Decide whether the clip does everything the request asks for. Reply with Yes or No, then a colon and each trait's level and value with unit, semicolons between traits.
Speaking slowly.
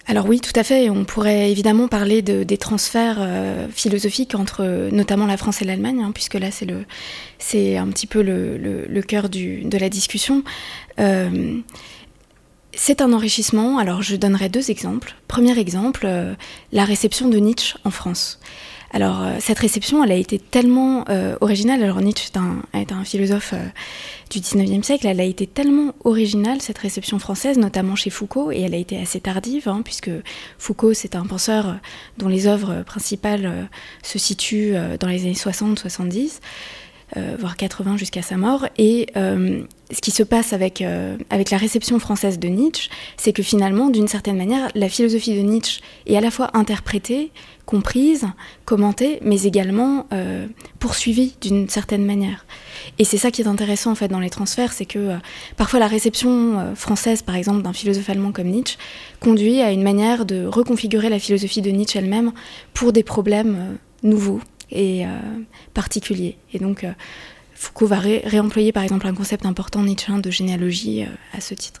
No: average, 185 wpm